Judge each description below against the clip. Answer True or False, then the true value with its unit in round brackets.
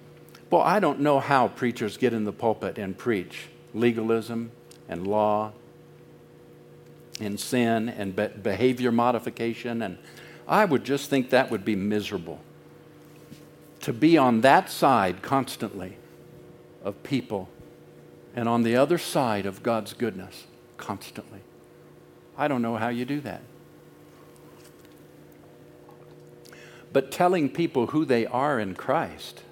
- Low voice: True (120 Hz)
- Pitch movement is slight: False (3.9 semitones)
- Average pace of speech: False (125 wpm)